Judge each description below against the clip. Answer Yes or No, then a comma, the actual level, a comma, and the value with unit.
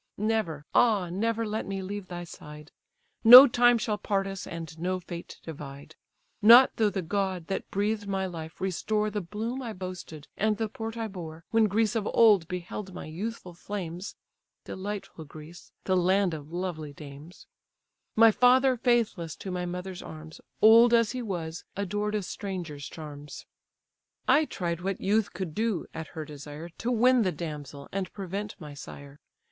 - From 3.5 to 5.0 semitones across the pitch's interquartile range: Yes, average, 4.7 semitones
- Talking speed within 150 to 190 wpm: Yes, average, 165 wpm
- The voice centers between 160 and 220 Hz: Yes, high, 190 Hz